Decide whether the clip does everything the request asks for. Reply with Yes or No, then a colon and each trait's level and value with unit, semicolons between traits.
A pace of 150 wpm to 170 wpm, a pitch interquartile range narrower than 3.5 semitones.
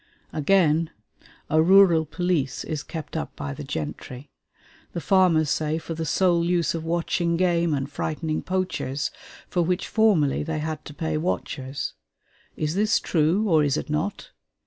Yes: average, 155 wpm; average, 2.8 semitones